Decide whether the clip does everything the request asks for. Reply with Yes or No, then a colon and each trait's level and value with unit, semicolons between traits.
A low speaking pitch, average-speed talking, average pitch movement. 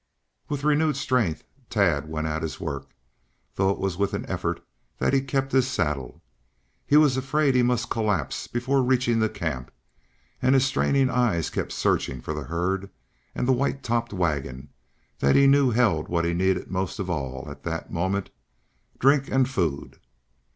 No: low, 100 Hz; average, 170 wpm; wide, 8.2 semitones